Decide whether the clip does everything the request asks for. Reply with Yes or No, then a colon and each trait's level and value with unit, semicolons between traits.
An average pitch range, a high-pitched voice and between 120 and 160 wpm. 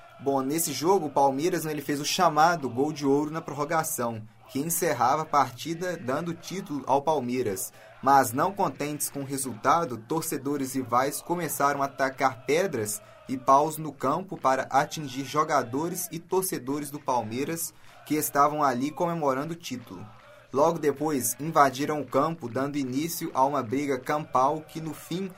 No: average, 3.2 semitones; medium, 145 Hz; average, 155 wpm